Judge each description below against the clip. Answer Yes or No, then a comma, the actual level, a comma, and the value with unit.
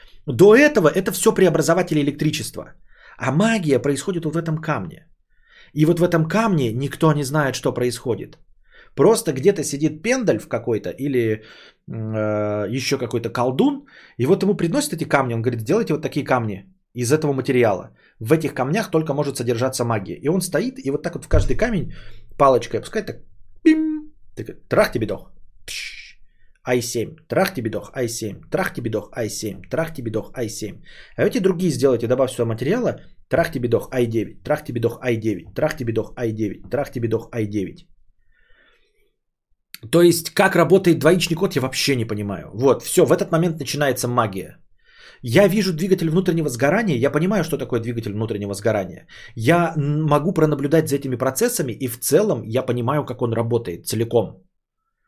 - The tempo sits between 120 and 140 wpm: No, average, 160 wpm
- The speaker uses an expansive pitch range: Yes, wide, 5.9 semitones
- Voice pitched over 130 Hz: Yes, medium, 140 Hz